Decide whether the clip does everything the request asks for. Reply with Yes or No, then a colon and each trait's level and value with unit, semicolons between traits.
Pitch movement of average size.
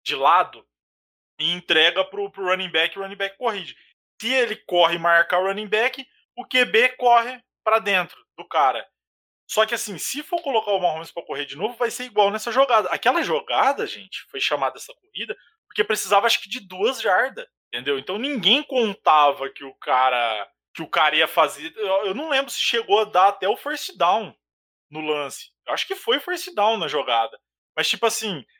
No: wide, 6.4 semitones